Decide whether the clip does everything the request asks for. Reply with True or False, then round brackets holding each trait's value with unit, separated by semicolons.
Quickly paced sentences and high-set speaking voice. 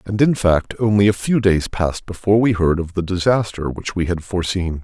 False (225 wpm; 95 Hz)